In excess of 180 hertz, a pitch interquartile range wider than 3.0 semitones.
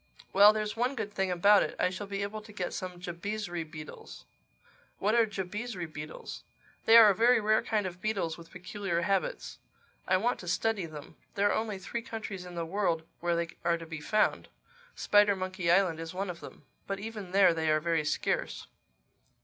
Yes: high, 190 Hz; average, 3.7 semitones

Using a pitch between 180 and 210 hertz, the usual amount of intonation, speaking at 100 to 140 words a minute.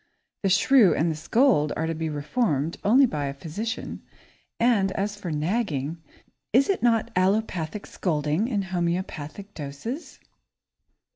No: medium, 185 Hz; wide, 6.3 semitones; slow, 135 wpm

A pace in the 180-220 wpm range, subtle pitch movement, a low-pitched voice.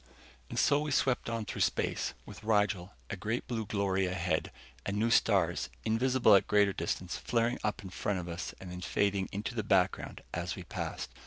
No: average, 190 wpm; average, 3.4 semitones; low, 100 Hz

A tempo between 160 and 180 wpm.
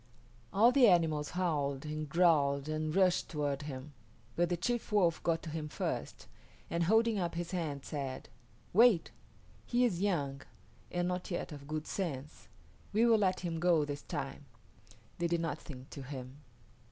Yes: average, 165 wpm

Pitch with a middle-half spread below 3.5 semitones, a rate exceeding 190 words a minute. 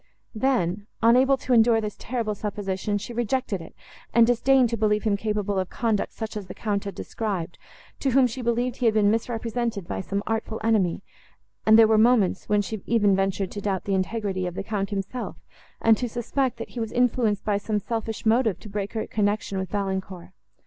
Yes: average, 2.7 semitones; average, 200 wpm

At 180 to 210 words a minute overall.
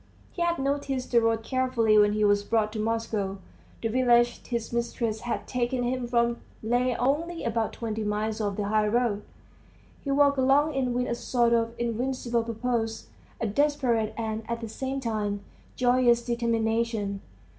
No: average, 165 wpm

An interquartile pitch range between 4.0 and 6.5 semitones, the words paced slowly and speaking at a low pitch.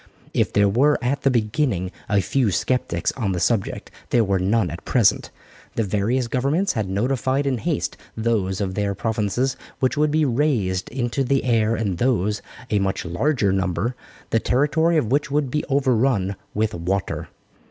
No: average, 5.3 semitones; average, 170 wpm; low, 115 Hz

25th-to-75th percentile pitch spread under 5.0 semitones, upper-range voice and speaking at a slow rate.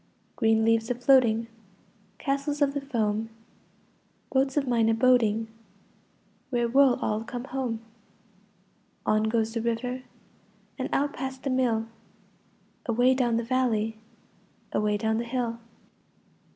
Yes: narrow, 2.6 semitones; high, 235 Hz; slow, 125 wpm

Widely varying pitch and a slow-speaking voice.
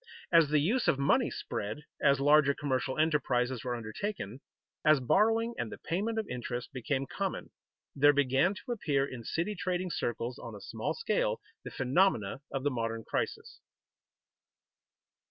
No: wide, 6.4 semitones; average, 155 wpm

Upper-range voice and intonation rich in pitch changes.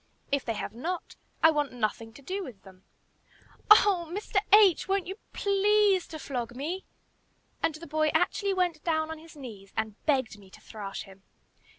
Yes: very high, 310 Hz; wide, 8.1 semitones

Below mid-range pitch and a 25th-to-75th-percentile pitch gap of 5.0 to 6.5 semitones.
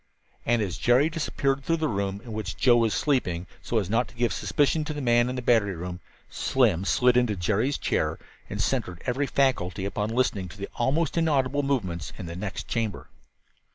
Yes: low, 120 Hz; average, 5.3 semitones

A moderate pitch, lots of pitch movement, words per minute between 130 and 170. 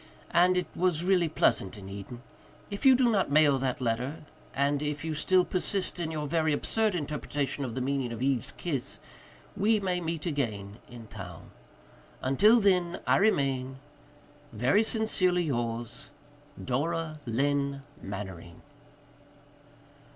Yes: medium, 145 Hz; wide, 6.3 semitones; slow, 135 wpm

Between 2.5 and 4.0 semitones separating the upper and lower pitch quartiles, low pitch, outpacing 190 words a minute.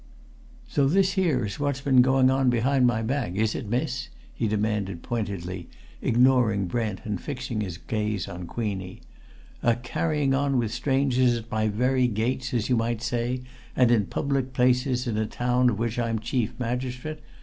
No: average, 3.1 semitones; low, 120 Hz; average, 170 wpm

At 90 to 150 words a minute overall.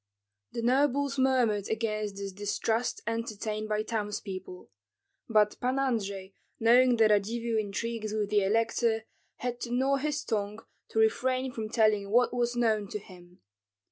Yes: average, 140 wpm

